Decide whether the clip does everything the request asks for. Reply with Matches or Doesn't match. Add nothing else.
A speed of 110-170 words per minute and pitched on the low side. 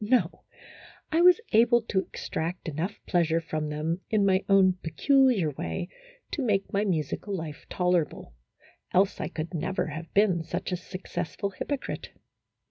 Doesn't match